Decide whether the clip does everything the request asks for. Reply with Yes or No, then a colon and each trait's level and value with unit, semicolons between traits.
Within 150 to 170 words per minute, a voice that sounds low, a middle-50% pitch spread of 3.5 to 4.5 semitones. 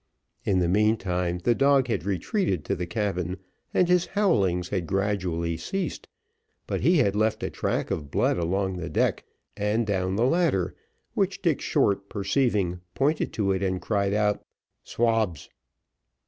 Yes: average, 155 wpm; low, 100 Hz; average, 3.9 semitones